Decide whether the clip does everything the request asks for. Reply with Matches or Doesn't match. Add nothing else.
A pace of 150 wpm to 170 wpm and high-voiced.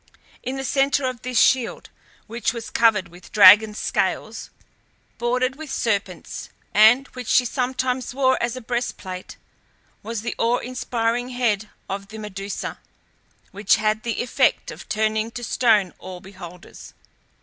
Doesn't match